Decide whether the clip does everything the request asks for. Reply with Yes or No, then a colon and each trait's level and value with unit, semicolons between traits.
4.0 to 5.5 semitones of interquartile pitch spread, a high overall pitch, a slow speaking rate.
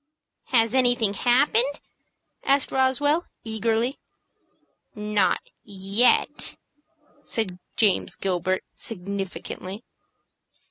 Yes: average, 4.4 semitones; high, 225 Hz; slow, 65 wpm